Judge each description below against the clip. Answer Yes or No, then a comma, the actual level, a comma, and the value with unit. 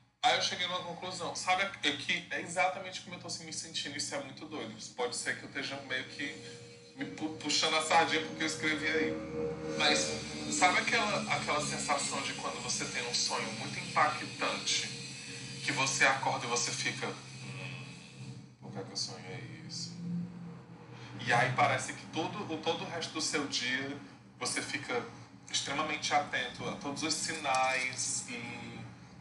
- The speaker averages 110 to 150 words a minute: No, average, 170 wpm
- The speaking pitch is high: No, medium, 150 Hz